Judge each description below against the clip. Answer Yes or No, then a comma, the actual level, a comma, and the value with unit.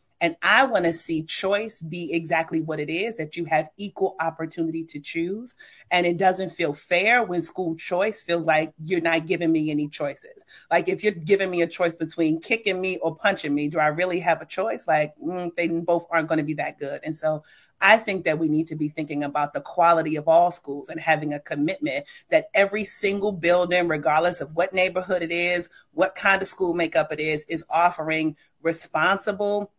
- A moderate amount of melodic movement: Yes, average, 3.0 semitones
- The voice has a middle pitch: Yes, medium, 170 Hz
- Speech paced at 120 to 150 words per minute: No, fast, 205 wpm